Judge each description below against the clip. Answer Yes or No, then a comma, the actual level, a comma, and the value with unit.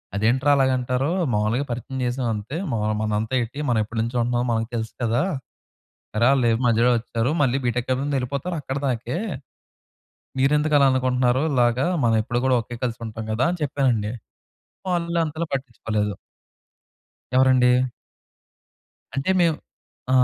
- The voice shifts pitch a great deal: No, average, 2.9 semitones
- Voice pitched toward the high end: No, low, 125 Hz